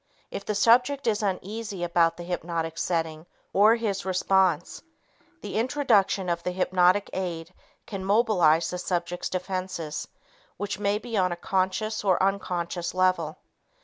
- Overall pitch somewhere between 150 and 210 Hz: Yes, medium, 185 Hz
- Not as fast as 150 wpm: Yes, average, 140 wpm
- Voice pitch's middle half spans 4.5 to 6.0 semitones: No, average, 2.8 semitones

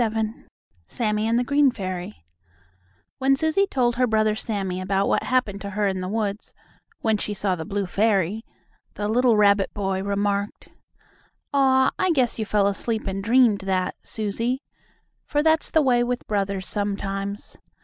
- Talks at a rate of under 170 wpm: Yes, average, 160 wpm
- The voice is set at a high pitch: Yes, high, 210 Hz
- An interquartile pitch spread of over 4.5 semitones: No, average, 3.6 semitones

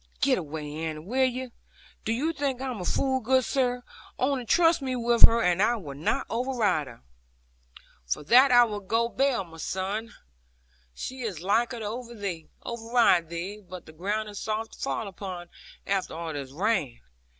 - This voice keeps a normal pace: Yes, average, 175 wpm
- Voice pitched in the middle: No, high, 220 Hz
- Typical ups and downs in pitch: No, wide, 5.9 semitones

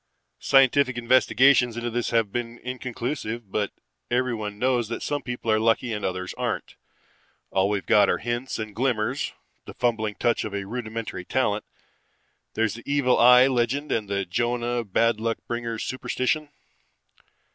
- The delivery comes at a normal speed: Yes, average, 150 wpm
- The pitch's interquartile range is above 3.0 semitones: No, average, 2.7 semitones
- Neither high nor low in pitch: No, low, 120 Hz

